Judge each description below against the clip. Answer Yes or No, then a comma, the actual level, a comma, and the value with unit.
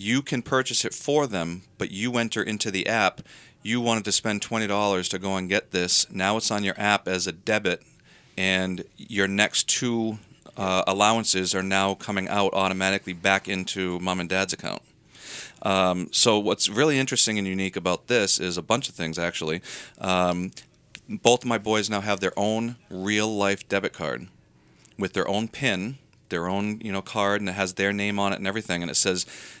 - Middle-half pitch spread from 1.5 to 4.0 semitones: Yes, average, 2.9 semitones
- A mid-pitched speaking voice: No, low, 100 Hz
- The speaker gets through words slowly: No, average, 195 wpm